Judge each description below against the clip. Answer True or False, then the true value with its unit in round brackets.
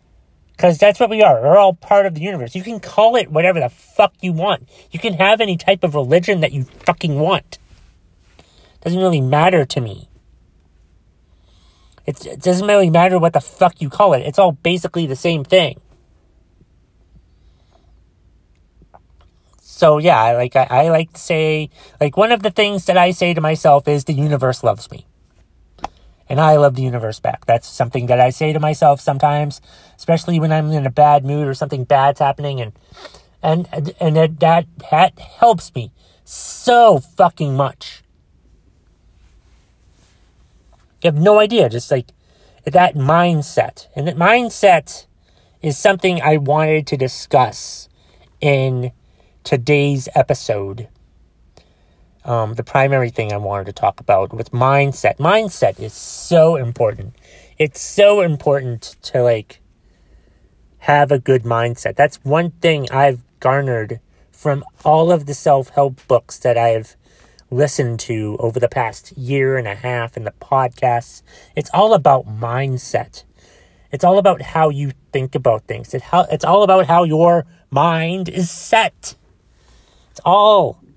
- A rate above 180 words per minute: False (155 wpm)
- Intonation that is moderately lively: False (7.8 semitones)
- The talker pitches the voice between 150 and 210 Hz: False (140 Hz)